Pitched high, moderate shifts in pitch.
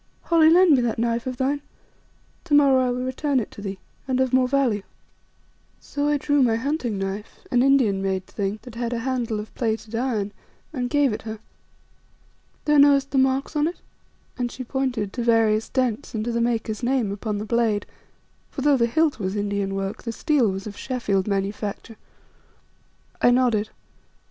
Yes: high, 240 Hz; average, 3.9 semitones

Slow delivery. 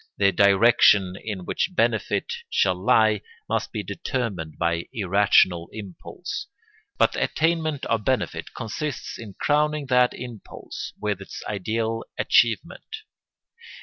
Yes: slow, 115 wpm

